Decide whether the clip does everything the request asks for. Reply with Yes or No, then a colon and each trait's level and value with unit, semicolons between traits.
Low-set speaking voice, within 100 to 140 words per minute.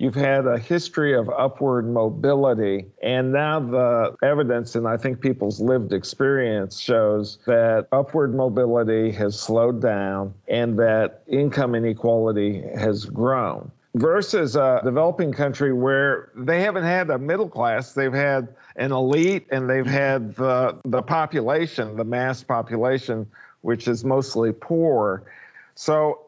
Yes: low, 125 Hz; slow, 135 wpm